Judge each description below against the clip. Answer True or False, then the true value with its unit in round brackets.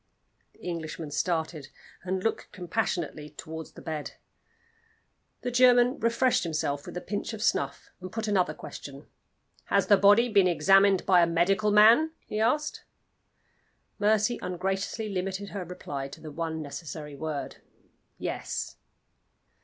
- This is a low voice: False (185 Hz)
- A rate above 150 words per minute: False (135 wpm)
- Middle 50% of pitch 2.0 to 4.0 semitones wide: False (4.9 semitones)